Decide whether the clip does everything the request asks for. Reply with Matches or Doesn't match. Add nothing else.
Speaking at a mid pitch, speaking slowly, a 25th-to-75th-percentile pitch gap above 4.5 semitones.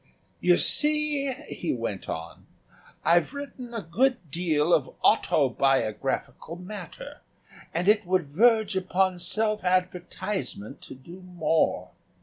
Matches